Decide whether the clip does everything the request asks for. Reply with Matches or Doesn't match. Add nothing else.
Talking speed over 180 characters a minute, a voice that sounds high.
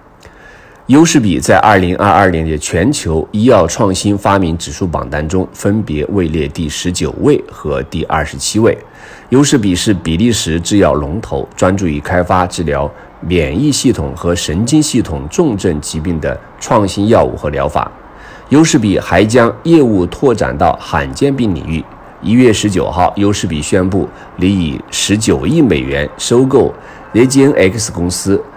Doesn't match